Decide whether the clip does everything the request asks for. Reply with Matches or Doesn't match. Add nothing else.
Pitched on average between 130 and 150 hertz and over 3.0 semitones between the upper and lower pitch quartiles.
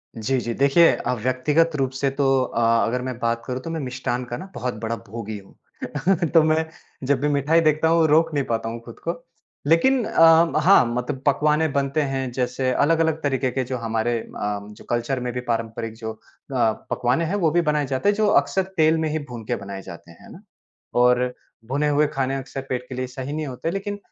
Matches